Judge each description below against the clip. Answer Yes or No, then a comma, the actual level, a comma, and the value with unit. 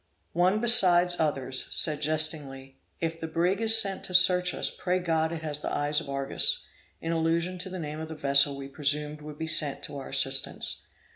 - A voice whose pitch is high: No, medium, 160 Hz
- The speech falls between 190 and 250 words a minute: Yes, fast, 205 wpm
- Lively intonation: No, average, 3.4 semitones